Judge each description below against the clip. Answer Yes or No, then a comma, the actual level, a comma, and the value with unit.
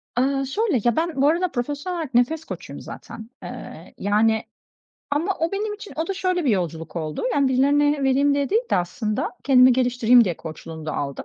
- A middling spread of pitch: No, wide, 6.4 semitones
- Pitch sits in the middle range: No, very high, 270 Hz